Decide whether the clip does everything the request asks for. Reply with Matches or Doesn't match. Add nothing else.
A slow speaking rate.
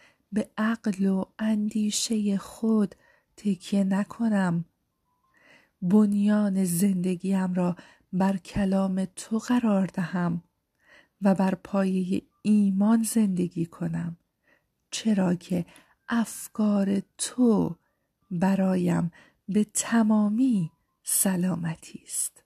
Matches